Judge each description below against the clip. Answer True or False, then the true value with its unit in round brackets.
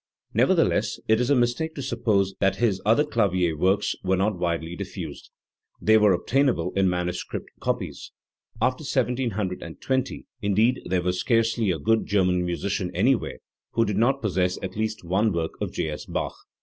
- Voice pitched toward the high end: False (100 Hz)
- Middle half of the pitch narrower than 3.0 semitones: False (4.6 semitones)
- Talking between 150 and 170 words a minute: True (165 wpm)